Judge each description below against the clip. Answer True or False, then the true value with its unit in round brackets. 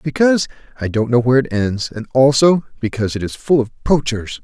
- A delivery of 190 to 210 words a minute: True (205 wpm)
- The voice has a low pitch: True (130 Hz)